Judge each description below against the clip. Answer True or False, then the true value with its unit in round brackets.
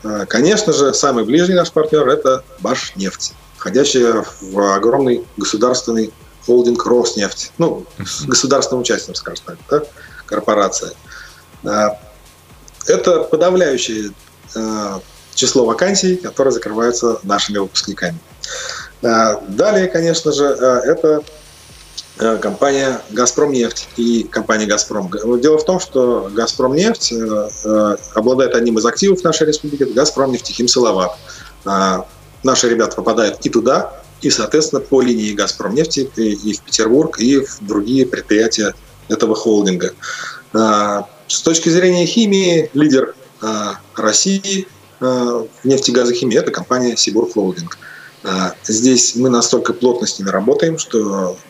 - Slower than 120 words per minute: True (110 wpm)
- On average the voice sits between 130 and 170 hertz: False (120 Hz)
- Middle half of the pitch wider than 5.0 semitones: False (4.7 semitones)